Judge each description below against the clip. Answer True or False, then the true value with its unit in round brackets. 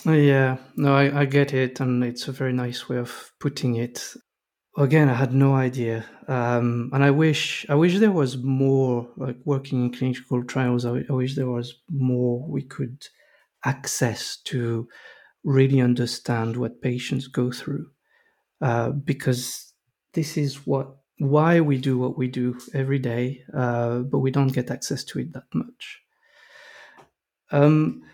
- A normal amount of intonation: False (2.2 semitones)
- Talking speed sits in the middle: True (160 wpm)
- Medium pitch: False (130 Hz)